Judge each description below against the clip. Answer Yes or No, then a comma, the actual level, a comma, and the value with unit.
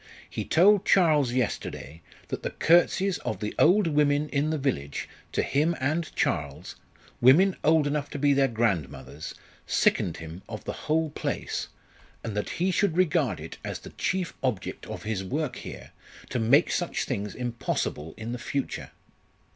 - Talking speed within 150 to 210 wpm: Yes, average, 165 wpm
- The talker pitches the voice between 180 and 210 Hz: No, medium, 140 Hz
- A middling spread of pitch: No, wide, 6.9 semitones